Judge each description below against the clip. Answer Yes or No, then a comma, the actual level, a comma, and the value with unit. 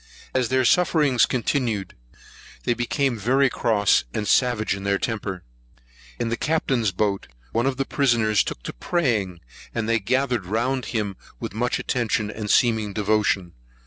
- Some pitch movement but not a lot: Yes, average, 3.8 semitones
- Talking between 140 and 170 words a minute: Yes, average, 150 wpm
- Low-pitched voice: Yes, low, 115 Hz